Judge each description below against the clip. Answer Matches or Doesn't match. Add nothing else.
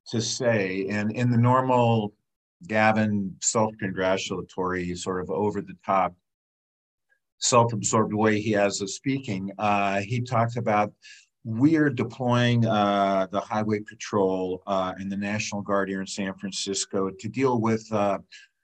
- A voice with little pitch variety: Doesn't match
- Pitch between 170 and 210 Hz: Doesn't match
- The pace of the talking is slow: Matches